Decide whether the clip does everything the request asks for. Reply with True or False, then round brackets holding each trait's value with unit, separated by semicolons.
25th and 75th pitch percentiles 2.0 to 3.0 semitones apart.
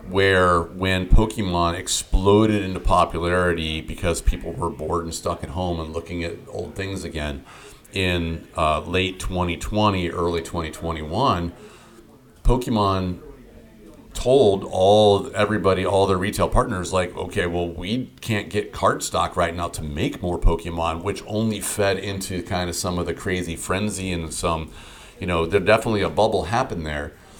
True (2.7 semitones)